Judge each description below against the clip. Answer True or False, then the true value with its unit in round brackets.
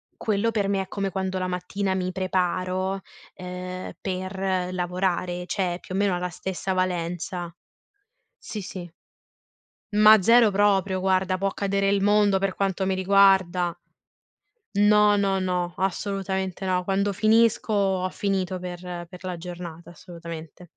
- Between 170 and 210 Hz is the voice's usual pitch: True (190 Hz)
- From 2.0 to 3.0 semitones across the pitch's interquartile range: False (1.6 semitones)